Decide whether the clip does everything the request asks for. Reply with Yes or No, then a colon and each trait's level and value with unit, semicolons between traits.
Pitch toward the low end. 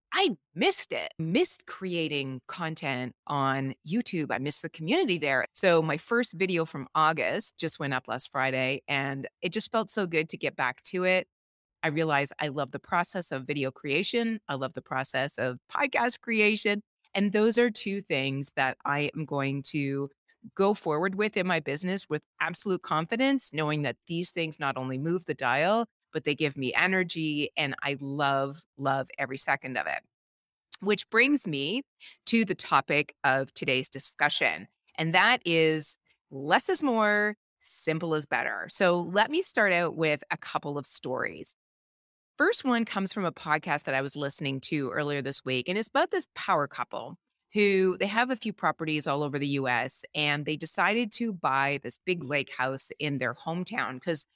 No: medium, 155 Hz